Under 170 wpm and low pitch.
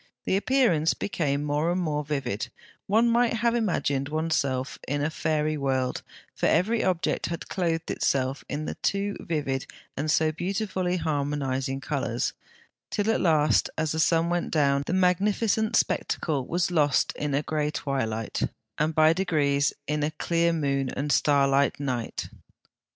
No: average, 150 wpm; medium, 155 Hz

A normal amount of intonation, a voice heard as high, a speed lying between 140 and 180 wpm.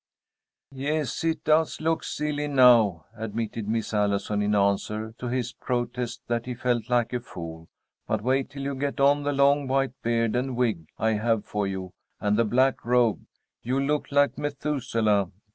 No: average, 4.3 semitones; low, 120 Hz; average, 170 wpm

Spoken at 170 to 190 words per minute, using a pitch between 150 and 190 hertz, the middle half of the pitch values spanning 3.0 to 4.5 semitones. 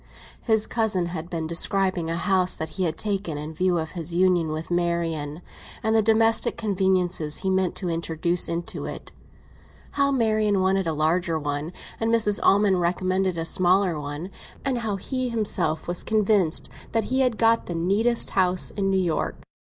Yes: average, 175 wpm; medium, 185 Hz; average, 3.9 semitones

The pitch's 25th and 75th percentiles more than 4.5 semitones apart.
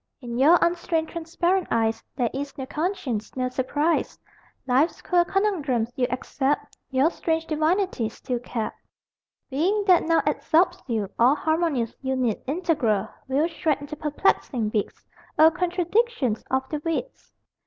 Yes: average, 5.2 semitones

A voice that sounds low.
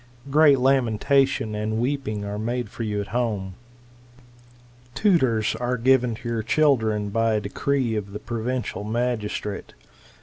Yes: low, 115 Hz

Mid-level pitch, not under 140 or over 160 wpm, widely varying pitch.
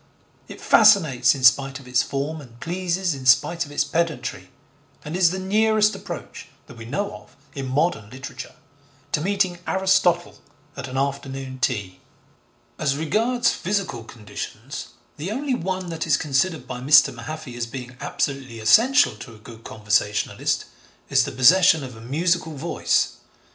Yes: medium, 145 Hz; average, 155 wpm; wide, 5.9 semitones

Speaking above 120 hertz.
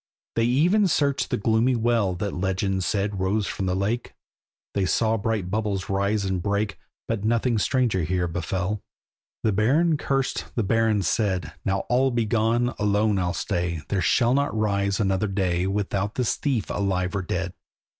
No: low, 105 Hz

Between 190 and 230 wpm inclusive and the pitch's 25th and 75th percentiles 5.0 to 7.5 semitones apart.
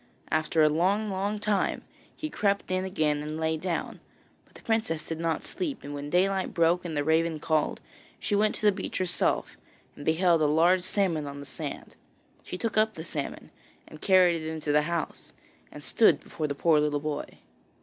No: average, 195 wpm; average, 3.7 semitones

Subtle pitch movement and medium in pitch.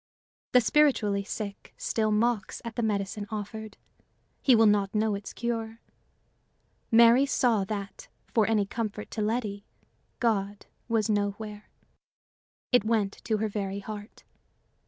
No: narrow, 2.0 semitones; high, 215 Hz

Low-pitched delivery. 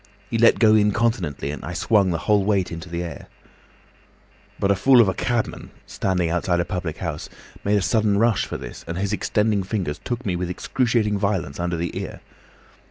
Yes: low, 100 Hz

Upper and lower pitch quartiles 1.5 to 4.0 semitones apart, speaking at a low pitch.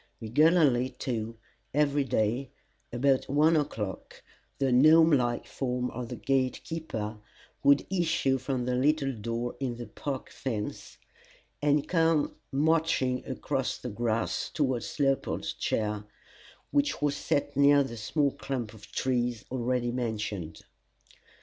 Yes: average, 3.4 semitones; low, 130 Hz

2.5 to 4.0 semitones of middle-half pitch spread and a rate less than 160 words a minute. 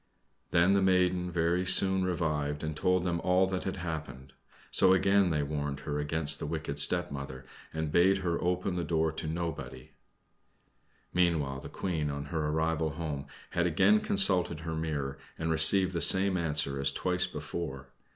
No: average, 3.5 semitones; average, 165 wpm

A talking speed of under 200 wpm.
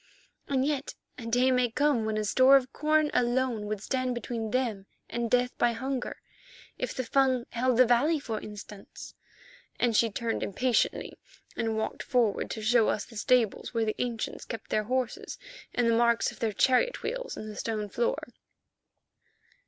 Yes: average, 170 wpm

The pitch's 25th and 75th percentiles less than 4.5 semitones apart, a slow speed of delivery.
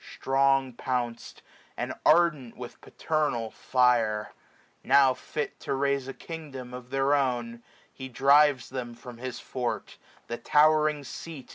Yes: average, 2.7 semitones; slow, 130 wpm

